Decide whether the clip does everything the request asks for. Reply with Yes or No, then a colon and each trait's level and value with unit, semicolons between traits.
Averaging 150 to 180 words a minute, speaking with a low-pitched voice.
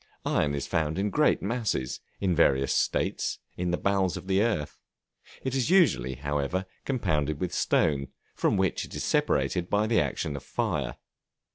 Yes: average, 165 wpm; very low, 90 Hz